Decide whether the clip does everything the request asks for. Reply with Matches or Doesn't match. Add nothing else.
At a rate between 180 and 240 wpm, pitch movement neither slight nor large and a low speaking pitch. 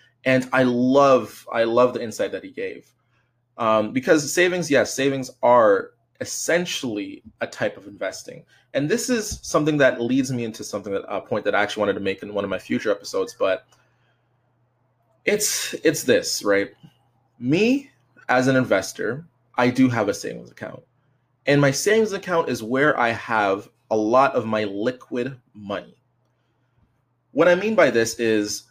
Doesn't match